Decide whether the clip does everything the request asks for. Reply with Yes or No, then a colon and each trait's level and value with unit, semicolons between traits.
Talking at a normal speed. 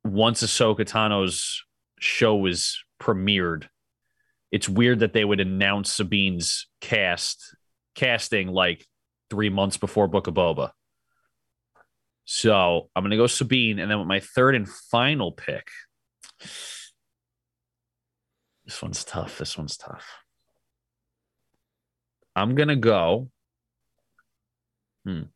No: slow, 105 wpm